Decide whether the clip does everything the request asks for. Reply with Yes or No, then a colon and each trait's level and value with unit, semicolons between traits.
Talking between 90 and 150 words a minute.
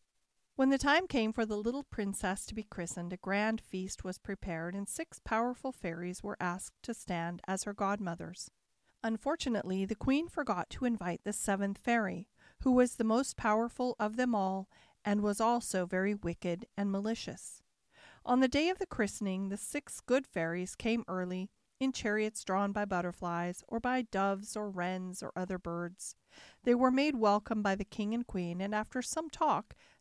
No: average, 180 wpm